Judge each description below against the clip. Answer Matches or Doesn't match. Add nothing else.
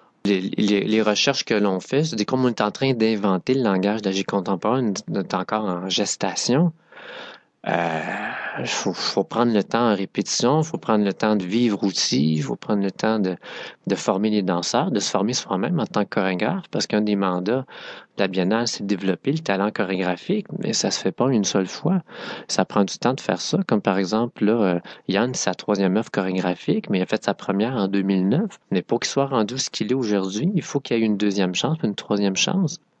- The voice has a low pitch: Matches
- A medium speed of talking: Doesn't match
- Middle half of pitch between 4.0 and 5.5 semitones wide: Matches